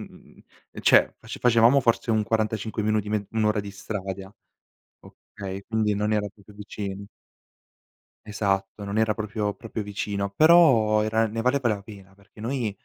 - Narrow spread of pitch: Yes, narrow, 1.7 semitones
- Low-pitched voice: Yes, low, 105 Hz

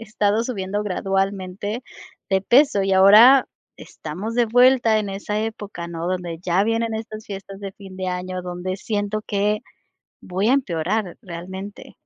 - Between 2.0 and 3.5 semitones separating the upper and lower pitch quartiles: Yes, average, 2.7 semitones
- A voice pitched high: Yes, high, 200 Hz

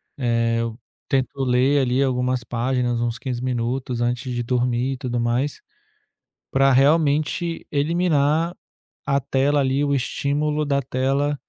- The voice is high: No, low, 130 Hz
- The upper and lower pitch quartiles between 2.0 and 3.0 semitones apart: Yes, narrow, 2.6 semitones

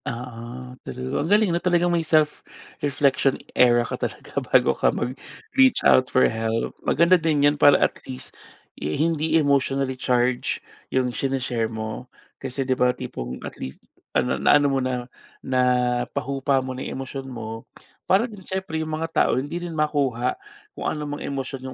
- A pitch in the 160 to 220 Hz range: No, low, 135 Hz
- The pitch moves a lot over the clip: No, average, 3.7 semitones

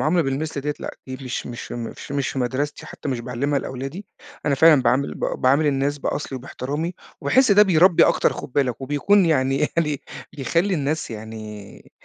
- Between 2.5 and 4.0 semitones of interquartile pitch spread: Yes, average, 3.4 semitones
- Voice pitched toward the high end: No, medium, 140 Hz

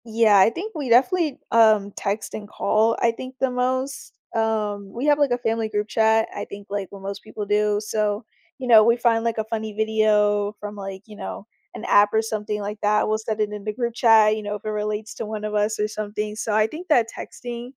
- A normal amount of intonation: No, narrow, 1.7 semitones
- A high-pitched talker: Yes, high, 215 Hz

